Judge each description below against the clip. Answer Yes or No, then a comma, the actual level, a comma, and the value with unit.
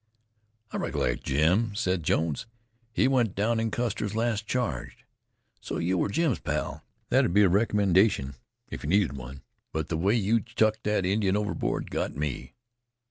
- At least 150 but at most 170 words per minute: Yes, average, 160 wpm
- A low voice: Yes, low, 100 Hz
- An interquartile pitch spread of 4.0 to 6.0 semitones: Yes, average, 5.1 semitones